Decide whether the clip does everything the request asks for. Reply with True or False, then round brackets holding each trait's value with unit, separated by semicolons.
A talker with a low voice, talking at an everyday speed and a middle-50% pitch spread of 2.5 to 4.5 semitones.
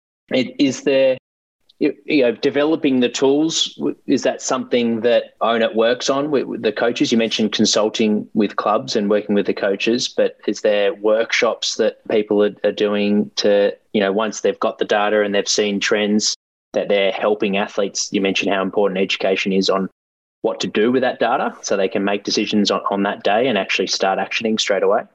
False (105 Hz; 185 wpm; 5.1 semitones)